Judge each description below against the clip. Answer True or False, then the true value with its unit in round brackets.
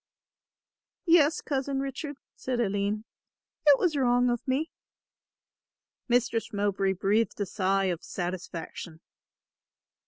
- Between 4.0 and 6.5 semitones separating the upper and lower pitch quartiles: True (5.6 semitones)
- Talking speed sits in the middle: False (100 wpm)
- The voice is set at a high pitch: True (230 Hz)